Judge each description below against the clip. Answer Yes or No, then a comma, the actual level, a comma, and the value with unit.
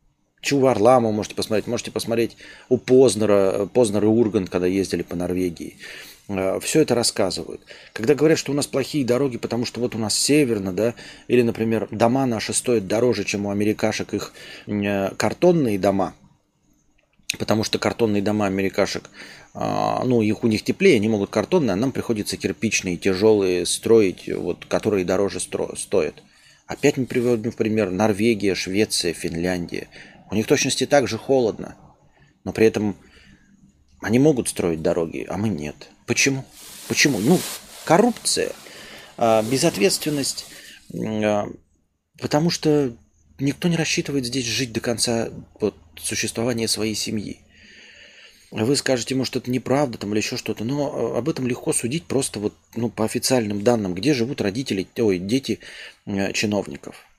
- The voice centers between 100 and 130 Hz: Yes, low, 110 Hz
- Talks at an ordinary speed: Yes, average, 140 wpm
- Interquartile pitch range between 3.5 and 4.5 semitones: Yes, average, 4.0 semitones